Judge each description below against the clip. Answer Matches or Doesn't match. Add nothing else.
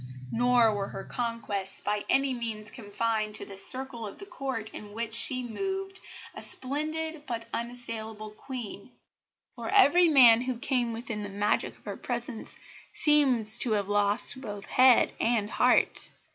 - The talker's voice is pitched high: Matches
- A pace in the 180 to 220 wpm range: Doesn't match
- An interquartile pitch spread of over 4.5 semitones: Doesn't match